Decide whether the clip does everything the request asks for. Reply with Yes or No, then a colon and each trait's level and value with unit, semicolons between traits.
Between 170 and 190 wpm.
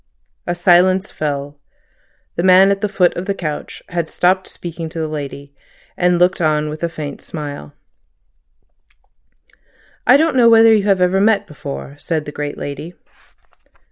No: average, 155 wpm